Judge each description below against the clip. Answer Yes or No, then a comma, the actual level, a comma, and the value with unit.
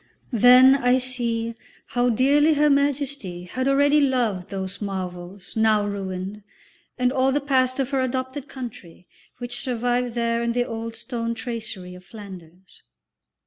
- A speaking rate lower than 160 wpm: Yes, average, 145 wpm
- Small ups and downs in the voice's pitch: No, average, 4.3 semitones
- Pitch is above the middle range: Yes, high, 240 Hz